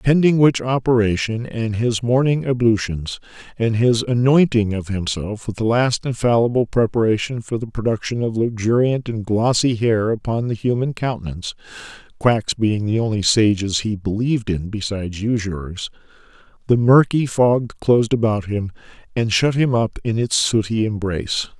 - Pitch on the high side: No, low, 115 Hz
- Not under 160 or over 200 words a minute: No, average, 145 wpm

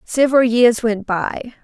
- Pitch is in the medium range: No, high, 235 Hz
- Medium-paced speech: Yes, average, 145 wpm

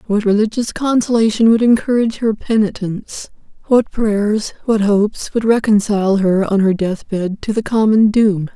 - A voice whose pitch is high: Yes, high, 210 Hz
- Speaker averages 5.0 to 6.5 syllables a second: No, 4.8 syllables/s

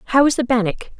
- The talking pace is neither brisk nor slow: No, fast, 240 wpm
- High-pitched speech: Yes, high, 240 Hz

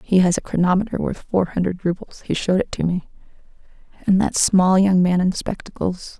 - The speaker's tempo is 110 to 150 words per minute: No, average, 195 wpm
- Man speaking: No, female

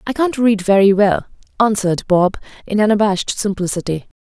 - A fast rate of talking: No, average, 140 wpm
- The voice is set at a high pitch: Yes, high, 205 Hz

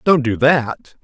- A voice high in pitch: No, low, 135 Hz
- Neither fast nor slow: Yes, average, 175 wpm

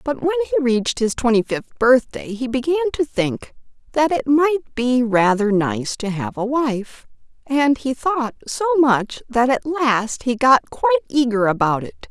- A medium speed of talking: Yes, average, 180 wpm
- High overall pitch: Yes, very high, 255 Hz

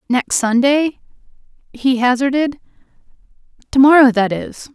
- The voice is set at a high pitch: Yes, very high, 260 Hz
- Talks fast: No, slow, 100 wpm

